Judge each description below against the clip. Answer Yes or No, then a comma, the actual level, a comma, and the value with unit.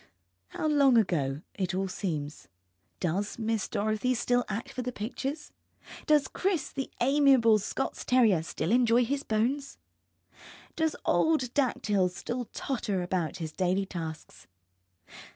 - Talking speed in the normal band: No, slow, 130 wpm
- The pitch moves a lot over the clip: Yes, wide, 6.2 semitones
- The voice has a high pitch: Yes, high, 225 Hz